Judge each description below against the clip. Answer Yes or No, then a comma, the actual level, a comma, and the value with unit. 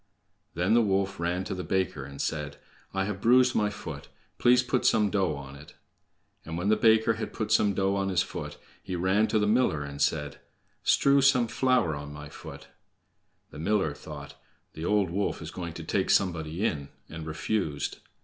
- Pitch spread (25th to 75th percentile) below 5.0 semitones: No, average, 5.3 semitones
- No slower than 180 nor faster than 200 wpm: Yes, average, 190 wpm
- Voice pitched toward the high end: No, very low, 95 Hz